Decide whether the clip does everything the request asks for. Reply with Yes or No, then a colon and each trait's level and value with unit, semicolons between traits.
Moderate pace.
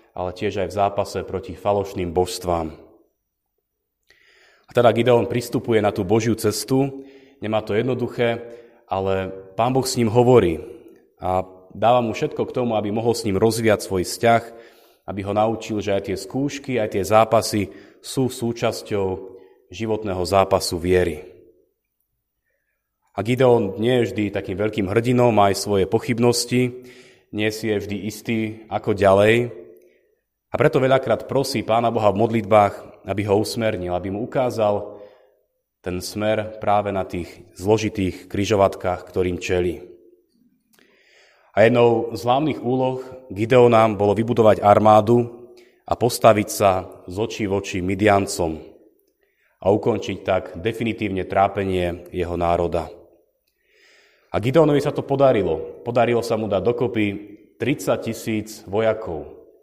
Yes: average, 135 wpm